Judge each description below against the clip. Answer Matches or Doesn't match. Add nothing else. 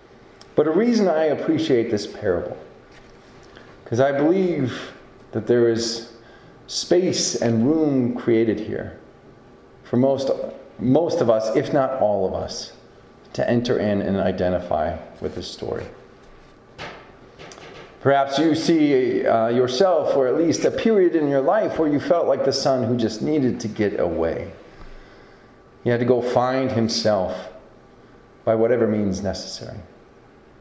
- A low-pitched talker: Matches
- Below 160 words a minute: Matches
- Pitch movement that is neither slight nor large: Matches